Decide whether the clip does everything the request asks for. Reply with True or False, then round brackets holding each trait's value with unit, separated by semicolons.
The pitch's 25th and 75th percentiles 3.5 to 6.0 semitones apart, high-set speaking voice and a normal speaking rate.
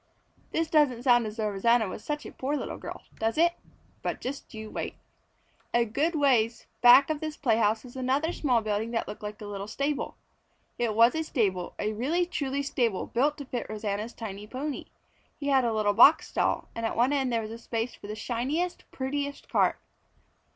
True (4.6 semitones; 240 Hz; 195 wpm)